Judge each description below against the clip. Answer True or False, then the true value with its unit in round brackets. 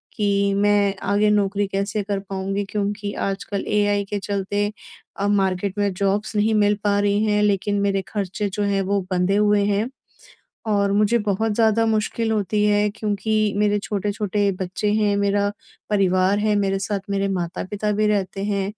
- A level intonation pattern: True (1.0 semitones)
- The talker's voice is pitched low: False (205 Hz)